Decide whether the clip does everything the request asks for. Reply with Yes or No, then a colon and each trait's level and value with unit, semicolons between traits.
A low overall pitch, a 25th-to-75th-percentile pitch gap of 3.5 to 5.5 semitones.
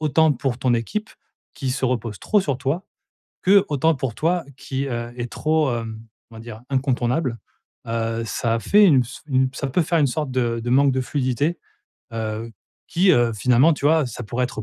Yes: low, 130 Hz; average, 4.4 semitones